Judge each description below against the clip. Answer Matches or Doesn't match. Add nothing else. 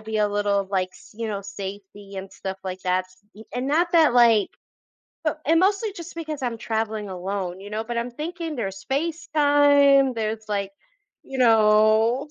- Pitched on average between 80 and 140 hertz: Doesn't match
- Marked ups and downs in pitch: Matches